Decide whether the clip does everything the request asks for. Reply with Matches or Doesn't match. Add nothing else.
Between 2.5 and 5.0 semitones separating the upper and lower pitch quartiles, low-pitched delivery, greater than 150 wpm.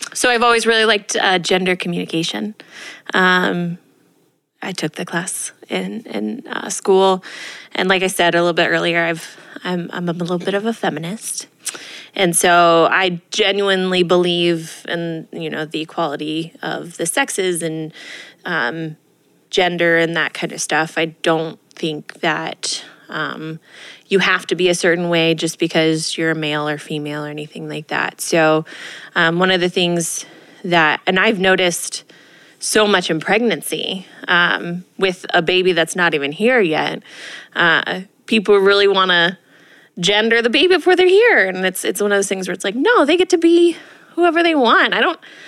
Doesn't match